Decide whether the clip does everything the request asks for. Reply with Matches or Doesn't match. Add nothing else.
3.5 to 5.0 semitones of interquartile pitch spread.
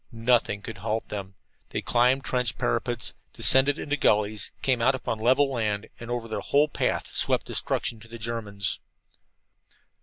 Doesn't match